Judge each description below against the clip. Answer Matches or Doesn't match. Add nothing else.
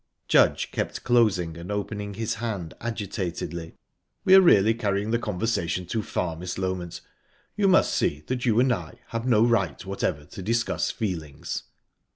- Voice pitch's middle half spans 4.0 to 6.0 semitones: Matches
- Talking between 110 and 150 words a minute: Doesn't match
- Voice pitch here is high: Doesn't match